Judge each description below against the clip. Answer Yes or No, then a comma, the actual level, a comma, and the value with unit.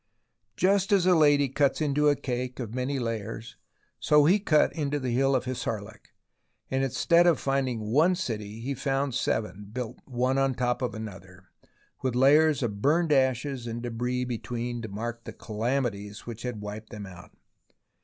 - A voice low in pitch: Yes, low, 125 Hz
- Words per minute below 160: No, average, 170 wpm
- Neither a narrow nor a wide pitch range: Yes, average, 3.8 semitones